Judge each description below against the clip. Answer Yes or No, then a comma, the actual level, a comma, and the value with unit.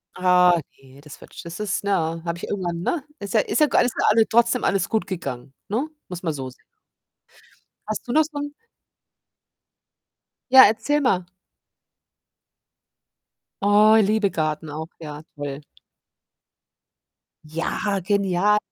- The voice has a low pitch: No, high, 190 Hz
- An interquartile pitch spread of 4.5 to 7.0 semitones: Yes, average, 5.1 semitones